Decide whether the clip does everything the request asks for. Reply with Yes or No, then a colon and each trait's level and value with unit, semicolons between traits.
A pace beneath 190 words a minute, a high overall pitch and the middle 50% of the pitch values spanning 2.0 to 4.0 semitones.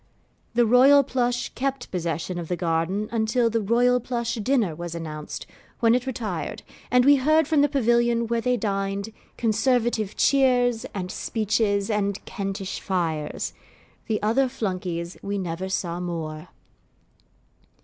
No: average, 140 wpm; high, 220 Hz; average, 5.0 semitones